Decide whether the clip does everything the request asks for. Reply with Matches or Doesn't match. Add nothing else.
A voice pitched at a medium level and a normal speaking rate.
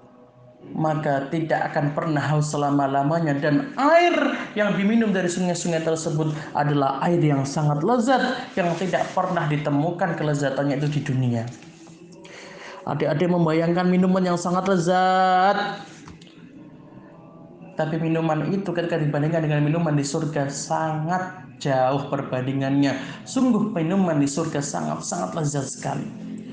Matches